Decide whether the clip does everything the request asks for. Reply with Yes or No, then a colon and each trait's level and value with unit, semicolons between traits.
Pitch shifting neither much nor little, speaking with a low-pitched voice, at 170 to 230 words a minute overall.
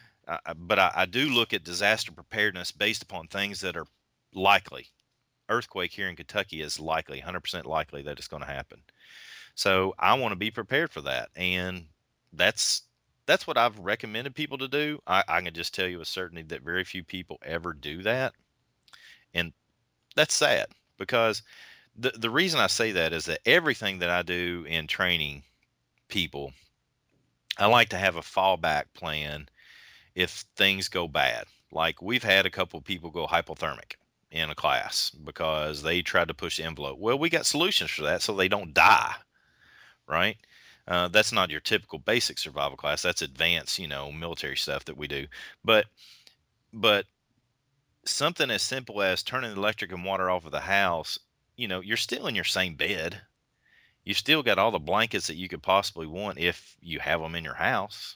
Yes: average, 3.8 semitones; very low, 90 Hz; average, 185 wpm